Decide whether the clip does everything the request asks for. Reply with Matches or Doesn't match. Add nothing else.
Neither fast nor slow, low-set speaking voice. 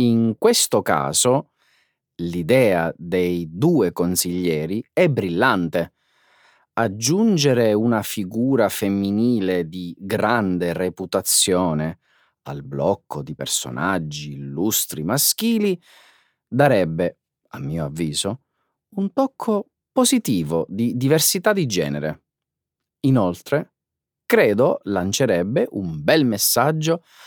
Doesn't match